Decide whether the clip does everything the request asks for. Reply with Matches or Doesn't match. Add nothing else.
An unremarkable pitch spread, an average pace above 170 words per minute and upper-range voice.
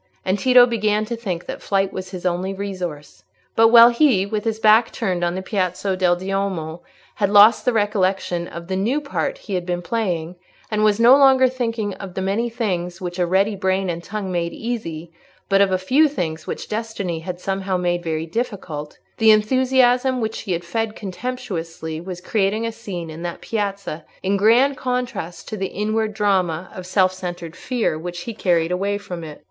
Matches